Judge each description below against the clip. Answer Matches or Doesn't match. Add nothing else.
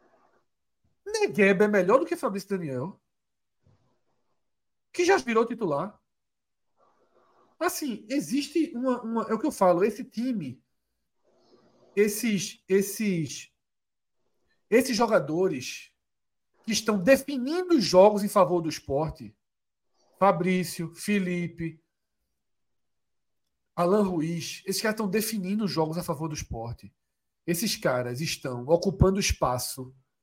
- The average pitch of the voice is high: Matches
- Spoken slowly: Matches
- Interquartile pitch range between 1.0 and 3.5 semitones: Doesn't match